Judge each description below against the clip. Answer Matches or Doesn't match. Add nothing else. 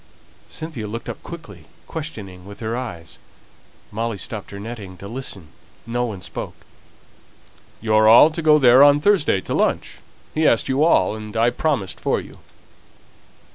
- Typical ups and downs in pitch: Doesn't match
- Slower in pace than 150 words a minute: Doesn't match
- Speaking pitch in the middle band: Doesn't match